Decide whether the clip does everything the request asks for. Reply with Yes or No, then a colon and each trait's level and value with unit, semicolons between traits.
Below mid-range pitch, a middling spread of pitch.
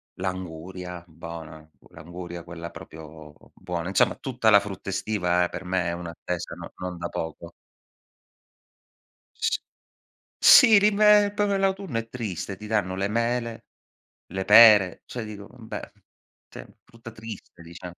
Yes: very low, 95 Hz; average, 4.8 semitones